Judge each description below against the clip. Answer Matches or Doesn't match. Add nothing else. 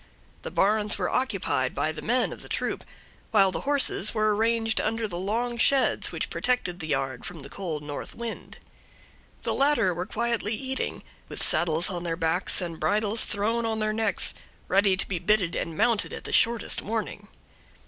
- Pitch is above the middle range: Matches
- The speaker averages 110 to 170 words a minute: Doesn't match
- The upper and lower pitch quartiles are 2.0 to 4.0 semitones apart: Doesn't match